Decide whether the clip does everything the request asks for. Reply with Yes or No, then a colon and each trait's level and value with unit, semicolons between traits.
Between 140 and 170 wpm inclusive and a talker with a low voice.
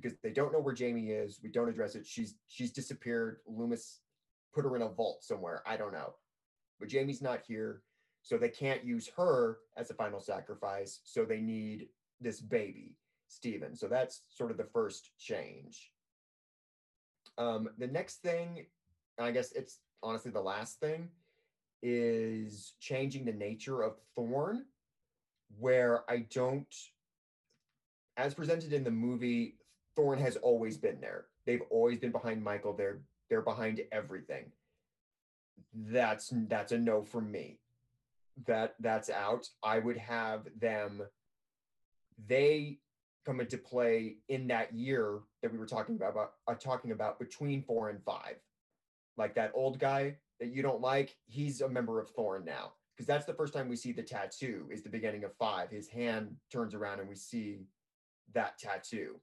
Yes: average, 160 wpm; low, 120 Hz